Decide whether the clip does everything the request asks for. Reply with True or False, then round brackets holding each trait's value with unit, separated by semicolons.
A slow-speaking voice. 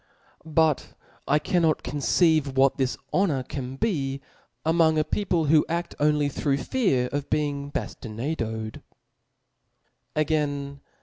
True (125 wpm)